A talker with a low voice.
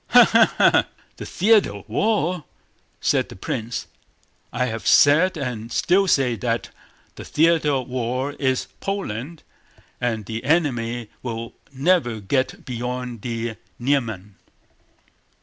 Yes: low, 125 Hz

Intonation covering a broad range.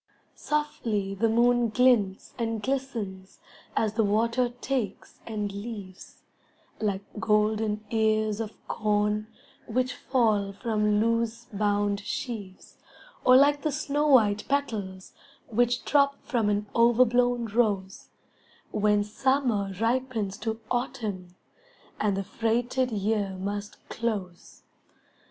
No: average, 2.9 semitones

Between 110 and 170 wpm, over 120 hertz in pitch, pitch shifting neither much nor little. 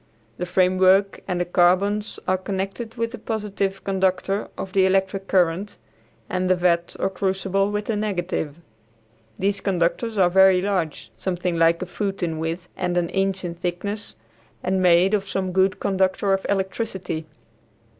No: average, 155 wpm; high, 190 Hz; narrow, 1.8 semitones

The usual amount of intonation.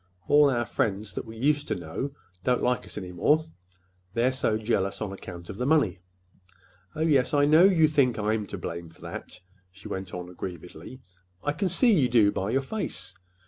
No: wide, 7.2 semitones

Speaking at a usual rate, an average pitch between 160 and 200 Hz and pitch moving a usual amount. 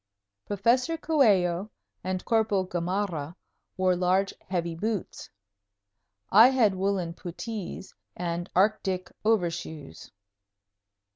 No: slow, 85 wpm; high, 190 Hz; average, 3.5 semitones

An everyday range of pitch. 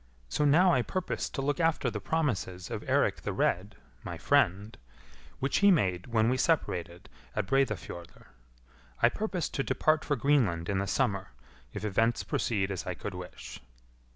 No: wide, 7.4 semitones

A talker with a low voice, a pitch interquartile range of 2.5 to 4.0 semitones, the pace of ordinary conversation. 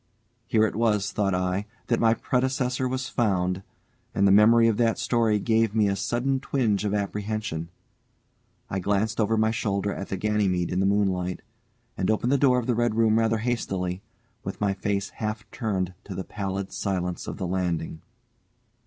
Yes: low, 105 Hz; average, 2.9 semitones; average, 180 wpm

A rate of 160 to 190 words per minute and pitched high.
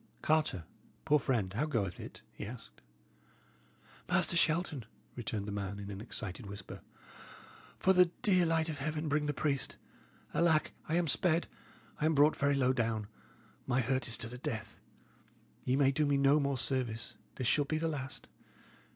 No: average, 170 wpm; low, 135 Hz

